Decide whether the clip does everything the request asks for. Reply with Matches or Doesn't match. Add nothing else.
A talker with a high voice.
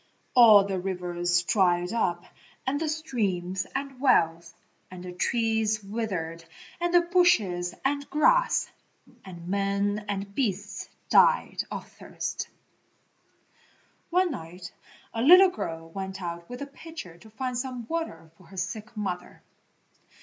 Matches